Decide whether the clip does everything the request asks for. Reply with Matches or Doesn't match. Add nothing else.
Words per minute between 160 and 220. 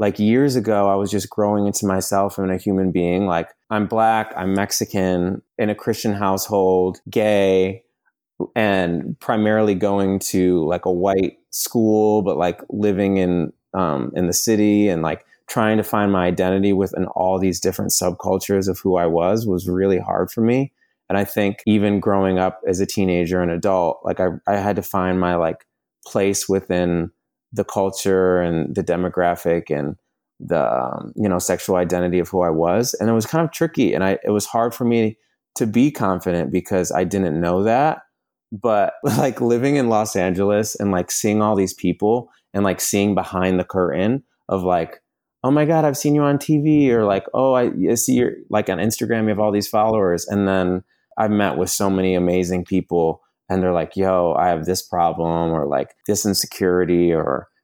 Matches